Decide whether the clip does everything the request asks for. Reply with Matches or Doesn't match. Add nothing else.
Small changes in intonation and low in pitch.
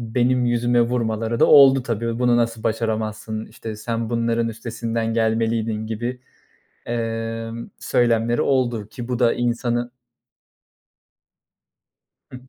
Matches